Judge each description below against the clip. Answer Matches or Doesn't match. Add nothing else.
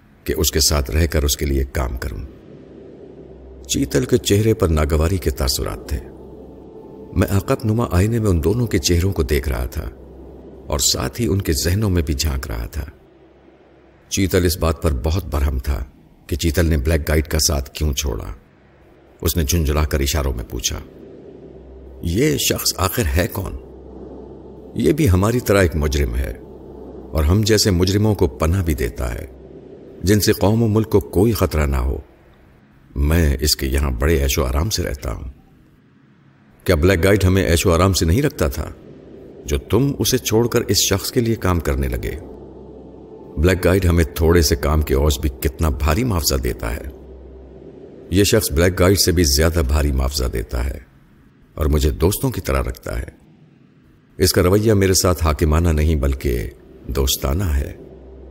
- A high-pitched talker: Doesn't match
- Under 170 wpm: Doesn't match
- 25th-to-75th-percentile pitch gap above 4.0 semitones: Matches